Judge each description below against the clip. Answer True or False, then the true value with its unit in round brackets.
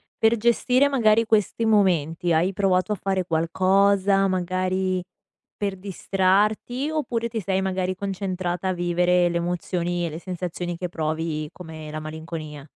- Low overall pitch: False (185 Hz)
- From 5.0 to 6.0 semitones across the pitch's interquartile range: False (2.6 semitones)